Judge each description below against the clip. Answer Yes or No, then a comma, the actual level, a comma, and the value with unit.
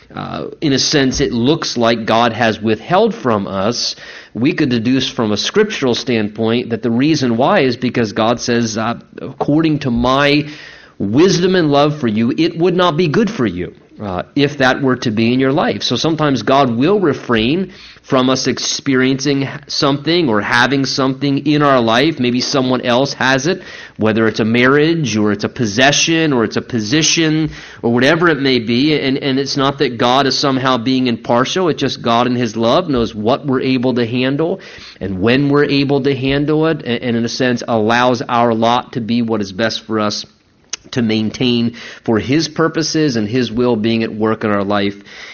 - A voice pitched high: No, low, 130 Hz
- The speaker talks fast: No, average, 195 wpm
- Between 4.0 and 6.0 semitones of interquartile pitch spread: No, average, 3.6 semitones